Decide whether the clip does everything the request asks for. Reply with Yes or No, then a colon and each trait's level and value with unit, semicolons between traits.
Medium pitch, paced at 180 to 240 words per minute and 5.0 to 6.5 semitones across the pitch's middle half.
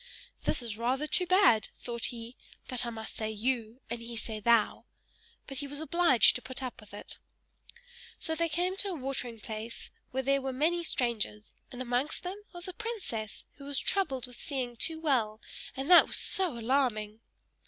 No: very high, 255 Hz; average, 190 wpm; average, 5.3 semitones